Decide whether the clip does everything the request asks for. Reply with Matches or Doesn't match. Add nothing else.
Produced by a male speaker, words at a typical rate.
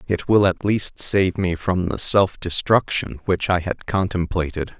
Matches